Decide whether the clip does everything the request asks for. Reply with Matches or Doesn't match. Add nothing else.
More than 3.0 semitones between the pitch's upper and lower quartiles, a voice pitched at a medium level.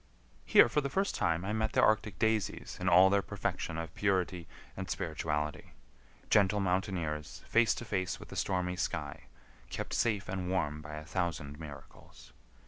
Doesn't match